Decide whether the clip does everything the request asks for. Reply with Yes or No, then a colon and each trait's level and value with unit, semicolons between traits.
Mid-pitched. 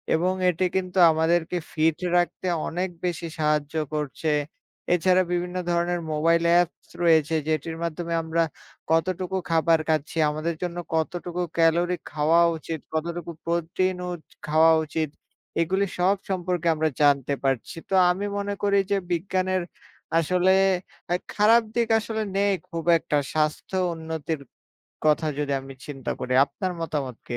Yes: medium, 170 Hz